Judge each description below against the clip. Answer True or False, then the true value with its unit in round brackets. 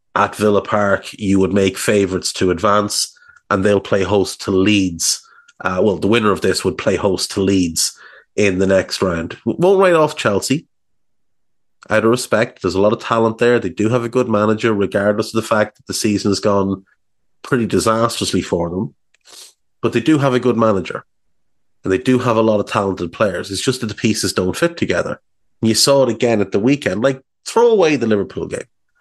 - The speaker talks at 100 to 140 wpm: False (205 wpm)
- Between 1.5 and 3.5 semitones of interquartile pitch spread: False (4.3 semitones)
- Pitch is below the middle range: True (110 Hz)